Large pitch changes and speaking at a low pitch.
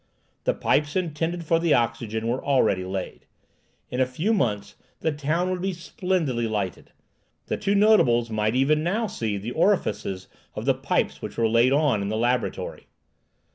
Yes: wide, 7.3 semitones; low, 130 Hz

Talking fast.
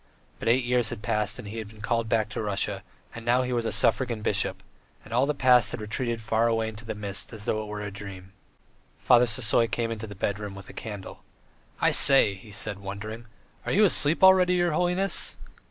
Yes: fast, 220 wpm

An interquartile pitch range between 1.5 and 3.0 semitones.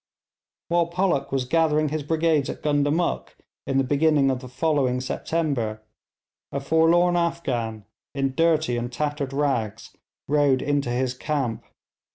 No: average, 3.8 semitones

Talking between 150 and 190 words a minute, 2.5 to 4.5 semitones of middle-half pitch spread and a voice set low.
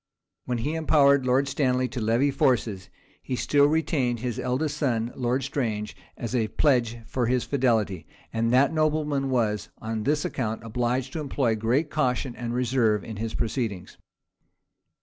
Yes: average, 155 wpm; average, 3.5 semitones; low, 125 Hz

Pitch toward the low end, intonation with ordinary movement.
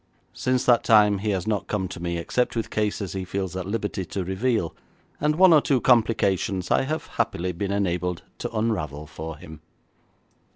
Yes: low, 100 Hz; average, 4.3 semitones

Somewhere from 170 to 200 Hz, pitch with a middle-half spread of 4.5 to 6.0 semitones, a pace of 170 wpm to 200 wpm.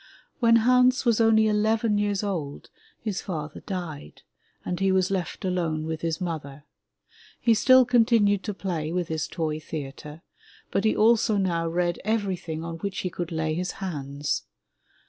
No: medium, 185 Hz; average, 5.0 semitones; average, 160 wpm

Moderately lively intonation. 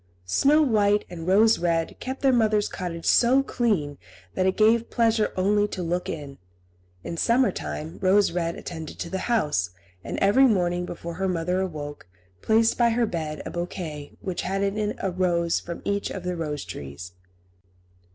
Yes: average, 4.5 semitones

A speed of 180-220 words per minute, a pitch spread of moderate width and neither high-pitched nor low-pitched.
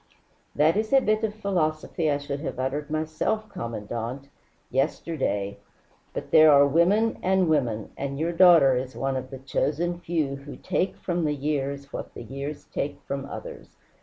No: average, 165 wpm; average, 3.9 semitones; medium, 145 Hz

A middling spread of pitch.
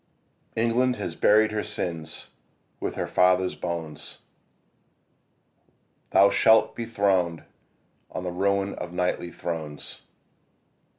Yes: average, 3.4 semitones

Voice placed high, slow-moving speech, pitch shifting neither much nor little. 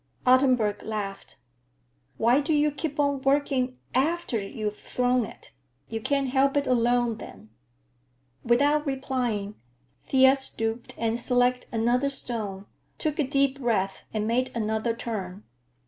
Yes: high, 245 Hz; slow, 130 wpm; average, 3.7 semitones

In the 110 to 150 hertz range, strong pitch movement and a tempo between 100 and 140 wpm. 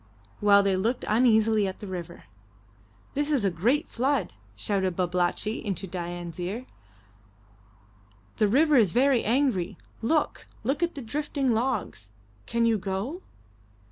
No: high, 220 Hz; wide, 5.8 semitones; slow, 135 wpm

